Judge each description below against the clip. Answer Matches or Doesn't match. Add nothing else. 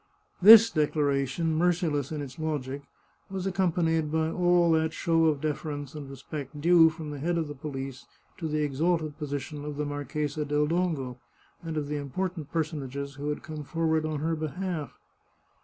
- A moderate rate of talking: Matches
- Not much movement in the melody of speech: Matches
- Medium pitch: Matches